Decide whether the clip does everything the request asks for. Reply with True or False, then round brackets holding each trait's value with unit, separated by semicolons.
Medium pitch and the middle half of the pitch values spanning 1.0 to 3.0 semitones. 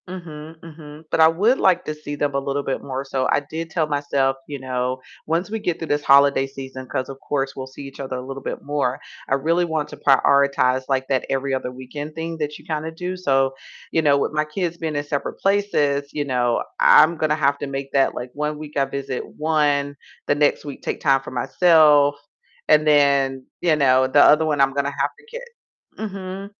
True (145 Hz; 2.6 semitones)